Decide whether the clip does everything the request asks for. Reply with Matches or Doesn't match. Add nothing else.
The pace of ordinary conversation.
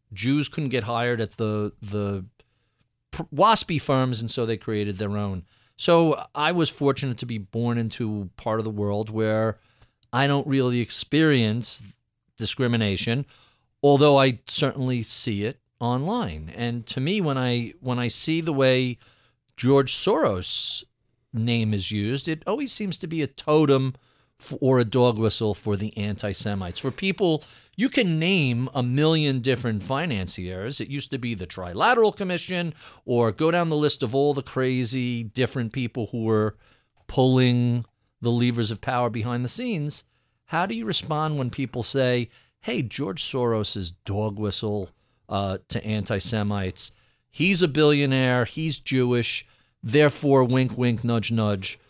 Matches